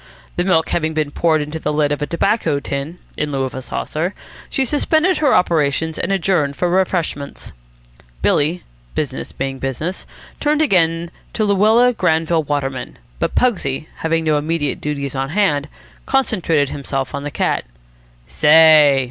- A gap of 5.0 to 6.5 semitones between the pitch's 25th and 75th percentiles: No, average, 4.1 semitones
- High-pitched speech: No, medium, 160 Hz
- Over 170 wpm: No, average, 155 wpm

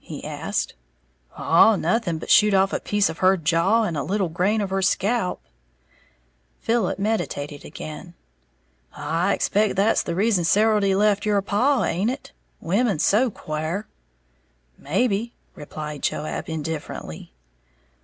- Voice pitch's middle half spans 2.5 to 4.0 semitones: No, average, 4.4 semitones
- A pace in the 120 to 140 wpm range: Yes, slow, 135 wpm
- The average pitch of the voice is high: Yes, high, 195 Hz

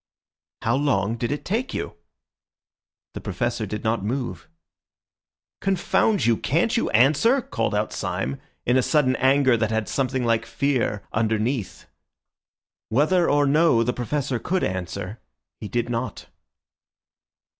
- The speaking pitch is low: Yes, low, 120 Hz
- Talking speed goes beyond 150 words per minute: No, slow, 135 wpm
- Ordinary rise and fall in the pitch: Yes, average, 4.5 semitones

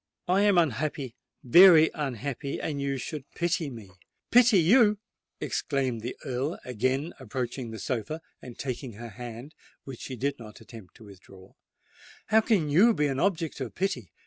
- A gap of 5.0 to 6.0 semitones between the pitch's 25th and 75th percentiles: Yes, wide, 5.5 semitones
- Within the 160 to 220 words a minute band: No, average, 150 wpm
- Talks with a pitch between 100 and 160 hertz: Yes, low, 135 Hz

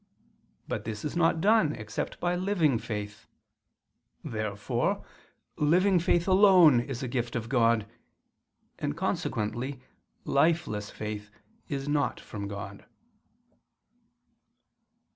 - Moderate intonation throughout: No, wide, 7.5 semitones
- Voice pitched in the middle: No, low, 130 Hz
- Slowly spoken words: Yes, slow, 105 wpm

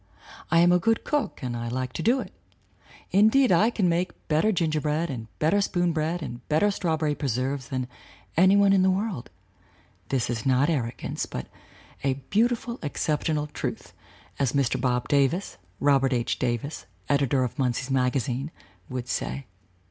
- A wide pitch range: Yes, wide, 5.7 semitones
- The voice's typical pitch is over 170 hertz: No, medium, 145 Hz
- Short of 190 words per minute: Yes, average, 160 wpm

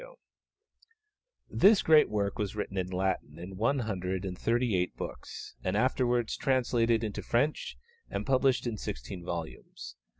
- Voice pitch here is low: Yes, low, 110 Hz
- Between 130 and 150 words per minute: Yes, average, 145 wpm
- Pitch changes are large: No, average, 4.9 semitones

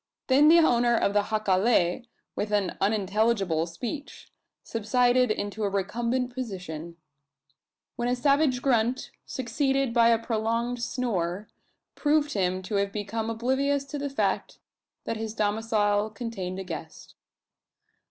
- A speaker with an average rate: No, slow, 130 wpm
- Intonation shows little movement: No, average, 3.7 semitones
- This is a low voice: No, high, 225 Hz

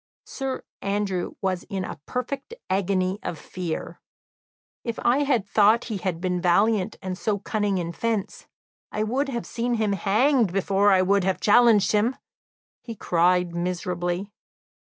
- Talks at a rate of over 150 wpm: No, average, 145 wpm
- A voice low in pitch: No, high, 200 Hz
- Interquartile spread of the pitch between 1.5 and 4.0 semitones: Yes, average, 3.6 semitones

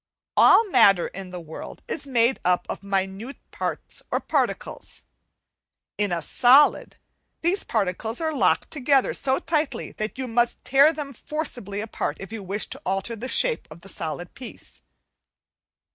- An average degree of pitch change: No, wide, 6.1 semitones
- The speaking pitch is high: Yes, high, 230 Hz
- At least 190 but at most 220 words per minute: No, average, 155 wpm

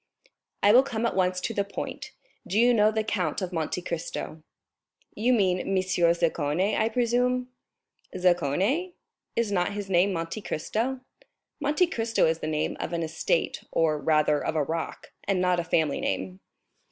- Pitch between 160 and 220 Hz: Yes, medium, 185 Hz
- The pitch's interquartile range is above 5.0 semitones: Yes, wide, 5.5 semitones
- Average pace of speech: Yes, average, 165 wpm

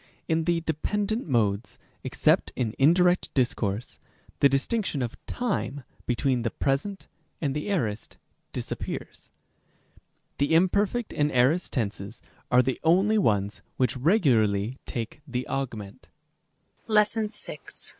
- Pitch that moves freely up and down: Yes, wide, 6.6 semitones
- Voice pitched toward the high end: No, low, 135 Hz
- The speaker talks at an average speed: No, slow, 120 wpm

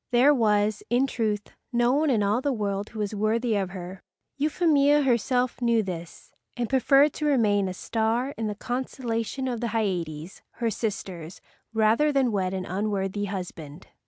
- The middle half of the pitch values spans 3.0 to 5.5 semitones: Yes, average, 4.0 semitones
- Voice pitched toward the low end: No, high, 220 Hz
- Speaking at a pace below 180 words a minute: Yes, average, 165 wpm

